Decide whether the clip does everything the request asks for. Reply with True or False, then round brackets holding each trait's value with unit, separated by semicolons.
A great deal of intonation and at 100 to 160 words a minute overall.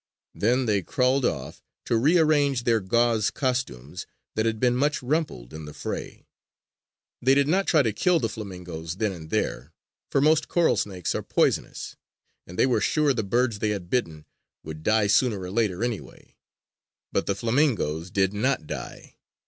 False (6.0 semitones; 170 wpm)